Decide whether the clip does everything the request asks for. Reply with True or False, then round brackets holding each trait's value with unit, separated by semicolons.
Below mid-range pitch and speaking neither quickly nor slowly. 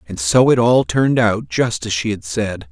False (110 Hz; 245 wpm)